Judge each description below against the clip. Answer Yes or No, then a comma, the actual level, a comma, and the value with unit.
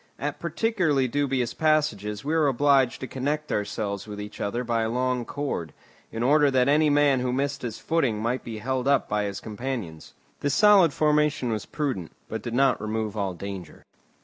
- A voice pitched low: Yes, low, 130 Hz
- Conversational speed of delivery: Yes, average, 185 wpm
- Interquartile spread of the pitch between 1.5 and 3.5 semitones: No, average, 5.0 semitones